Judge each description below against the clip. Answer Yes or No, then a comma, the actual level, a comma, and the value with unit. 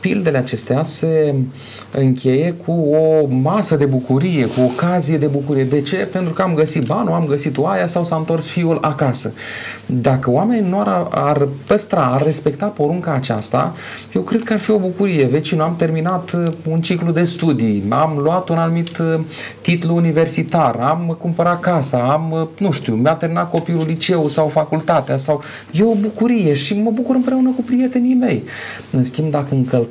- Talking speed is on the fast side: Yes, fast, 175 wpm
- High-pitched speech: No, medium, 160 Hz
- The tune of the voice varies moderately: Yes, average, 3.9 semitones